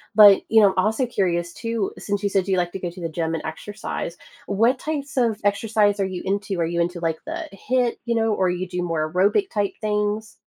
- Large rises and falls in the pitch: No, average, 3.8 semitones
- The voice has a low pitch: No, high, 200 Hz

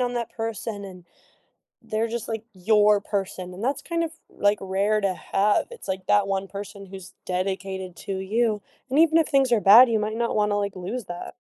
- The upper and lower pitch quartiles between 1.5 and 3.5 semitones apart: Yes, average, 2.9 semitones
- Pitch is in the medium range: No, high, 205 Hz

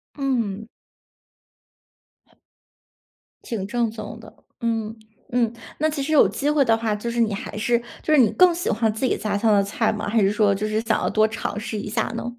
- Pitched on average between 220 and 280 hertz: Yes, high, 225 Hz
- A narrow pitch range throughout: Yes, narrow, 2.2 semitones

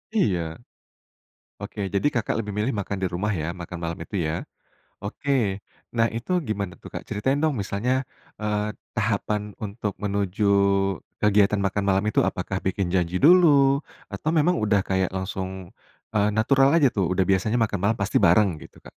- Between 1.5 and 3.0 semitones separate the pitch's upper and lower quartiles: Yes, narrow, 2.5 semitones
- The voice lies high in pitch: No, low, 105 Hz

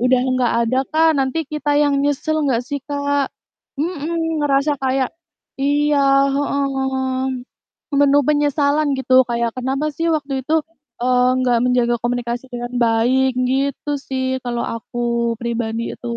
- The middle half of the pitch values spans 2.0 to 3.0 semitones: Yes, narrow, 2.6 semitones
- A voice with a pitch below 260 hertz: No, very high, 265 Hz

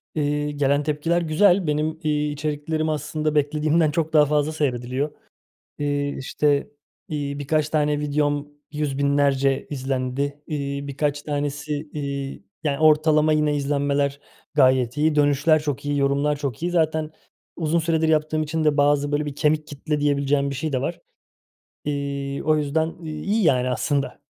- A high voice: No, medium, 145 Hz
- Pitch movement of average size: No, narrow, 1.5 semitones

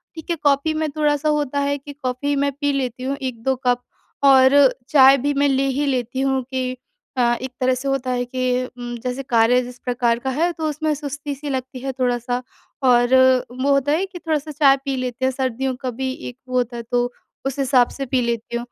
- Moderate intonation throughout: No, narrow, 2.2 semitones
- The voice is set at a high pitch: Yes, very high, 265 Hz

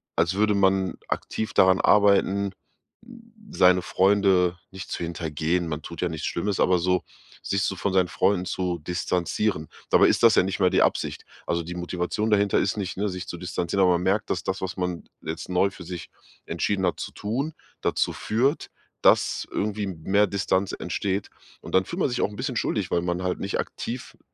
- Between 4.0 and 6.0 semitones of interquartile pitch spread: No, narrow, 2.4 semitones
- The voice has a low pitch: Yes, very low, 95 Hz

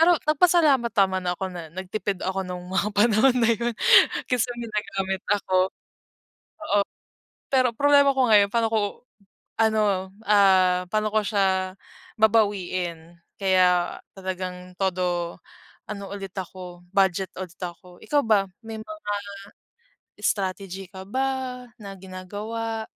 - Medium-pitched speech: No, high, 200 Hz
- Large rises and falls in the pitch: No, average, 3.4 semitones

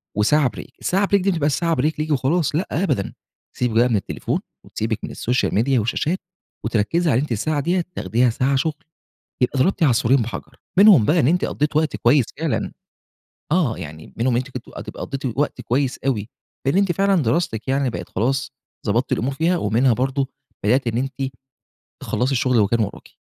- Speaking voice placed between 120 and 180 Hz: Yes, low, 135 Hz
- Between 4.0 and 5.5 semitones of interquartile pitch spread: Yes, average, 5.0 semitones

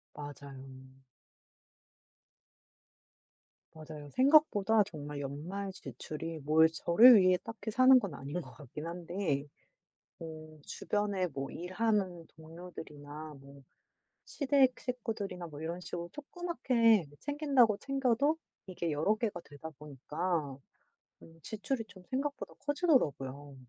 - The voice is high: No, medium, 175 Hz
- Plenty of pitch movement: Yes, wide, 7.2 semitones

